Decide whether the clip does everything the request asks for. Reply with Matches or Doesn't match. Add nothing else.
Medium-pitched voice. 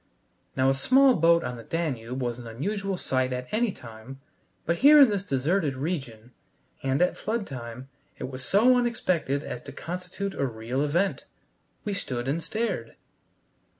Matches